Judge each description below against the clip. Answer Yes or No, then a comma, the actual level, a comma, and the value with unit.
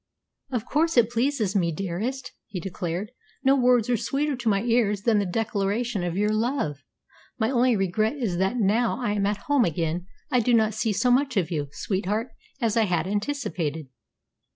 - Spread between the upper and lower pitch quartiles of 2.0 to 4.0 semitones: No, average, 4.4 semitones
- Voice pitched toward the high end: Yes, high, 215 Hz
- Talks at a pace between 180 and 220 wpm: Yes, average, 185 wpm